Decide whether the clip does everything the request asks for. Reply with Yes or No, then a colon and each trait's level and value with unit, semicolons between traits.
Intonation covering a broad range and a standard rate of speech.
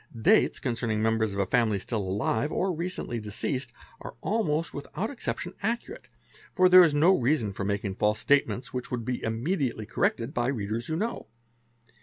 Yes: wide, 7.3 semitones; average, 170 wpm